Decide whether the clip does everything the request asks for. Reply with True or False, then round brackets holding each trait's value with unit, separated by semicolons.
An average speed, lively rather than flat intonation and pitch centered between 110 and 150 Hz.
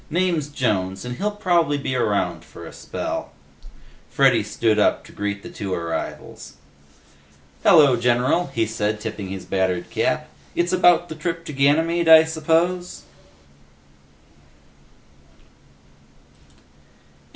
False (120 wpm; 7.9 semitones; 140 Hz)